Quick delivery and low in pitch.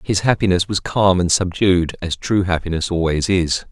No: average, 175 wpm; very low, 90 Hz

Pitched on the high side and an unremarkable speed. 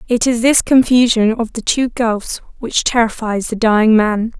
Yes: high, 230 Hz; average, 180 wpm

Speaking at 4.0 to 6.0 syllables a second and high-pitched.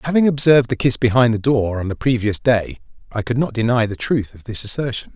No: 5.9 syllables/s; low, 120 Hz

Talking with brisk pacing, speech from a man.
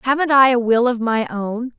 No: fast, 235 wpm; female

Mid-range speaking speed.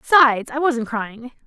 Yes: average, 165 wpm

